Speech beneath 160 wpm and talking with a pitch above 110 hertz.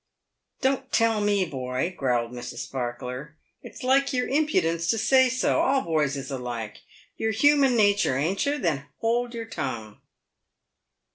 Yes: average, 145 wpm; high, 190 Hz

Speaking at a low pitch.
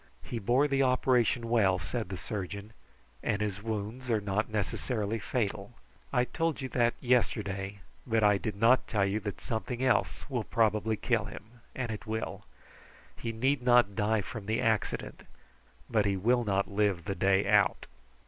Yes: low, 110 Hz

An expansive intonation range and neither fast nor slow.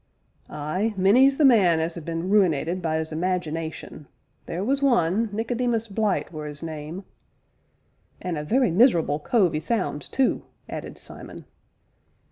Yes: wide, 6.0 semitones; average, 145 wpm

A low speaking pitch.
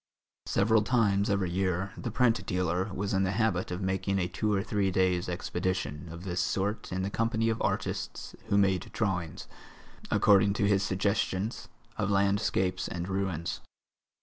Yes: very low, 95 Hz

